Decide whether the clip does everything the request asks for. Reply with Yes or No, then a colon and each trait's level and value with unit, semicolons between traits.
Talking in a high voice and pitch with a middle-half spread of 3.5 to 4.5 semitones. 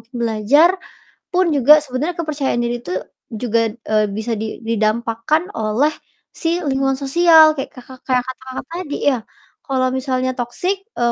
Yes: very high, 260 Hz; average, 4.0 semitones